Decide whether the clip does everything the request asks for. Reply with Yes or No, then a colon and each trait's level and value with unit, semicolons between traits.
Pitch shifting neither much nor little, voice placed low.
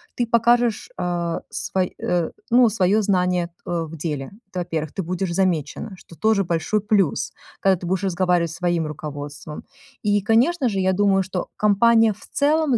No: average, 4.0 semitones; medium, 185 Hz